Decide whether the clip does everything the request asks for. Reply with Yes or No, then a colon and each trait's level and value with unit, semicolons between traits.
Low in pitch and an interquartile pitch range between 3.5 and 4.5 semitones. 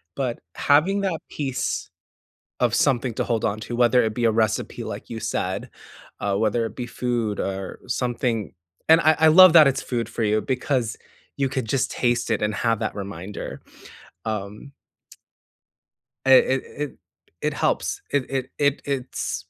Yes: low, 120 Hz; average, 3.8 semitones